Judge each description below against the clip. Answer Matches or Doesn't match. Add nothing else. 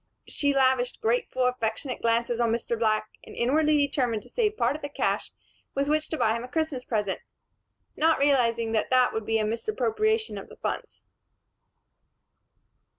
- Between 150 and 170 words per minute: Matches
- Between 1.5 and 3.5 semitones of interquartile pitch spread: Doesn't match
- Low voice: Doesn't match